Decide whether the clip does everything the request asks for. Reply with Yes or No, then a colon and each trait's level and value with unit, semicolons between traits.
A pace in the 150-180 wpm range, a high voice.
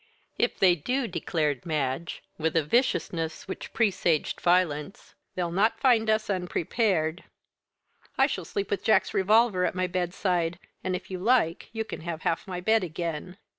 No: average, 160 wpm; medium, 180 Hz